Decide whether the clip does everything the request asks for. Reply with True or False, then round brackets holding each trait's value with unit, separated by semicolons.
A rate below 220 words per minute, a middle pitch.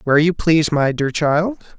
True (200 wpm; 155 Hz)